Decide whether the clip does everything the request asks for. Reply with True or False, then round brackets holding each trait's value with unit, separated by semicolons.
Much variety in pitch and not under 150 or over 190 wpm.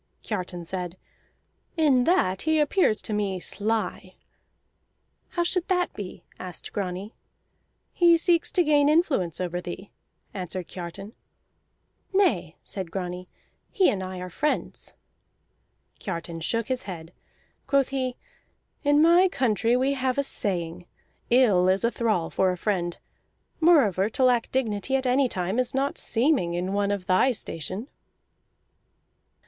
False (7.0 semitones; 135 wpm)